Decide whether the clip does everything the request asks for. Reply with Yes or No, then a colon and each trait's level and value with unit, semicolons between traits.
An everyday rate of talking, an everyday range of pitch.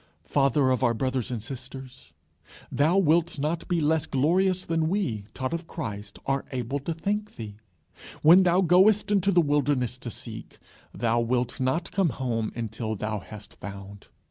No: average, 165 wpm; wide, 6.2 semitones